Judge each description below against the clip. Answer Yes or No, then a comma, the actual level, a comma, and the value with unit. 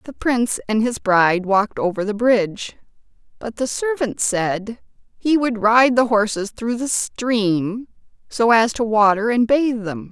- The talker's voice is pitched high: Yes, high, 225 Hz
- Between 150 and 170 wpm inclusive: Yes, average, 165 wpm